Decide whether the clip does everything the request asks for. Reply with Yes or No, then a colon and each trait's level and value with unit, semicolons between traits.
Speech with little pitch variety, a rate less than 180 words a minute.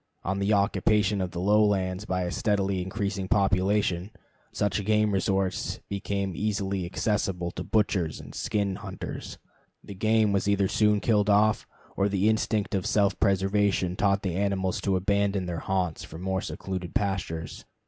Yes: narrow, 1.6 semitones; average, 155 wpm